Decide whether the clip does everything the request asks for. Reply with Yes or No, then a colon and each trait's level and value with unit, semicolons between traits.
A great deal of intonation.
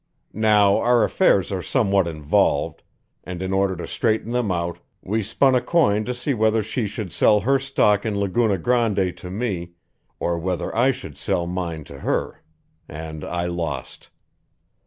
No: average, 4.8 semitones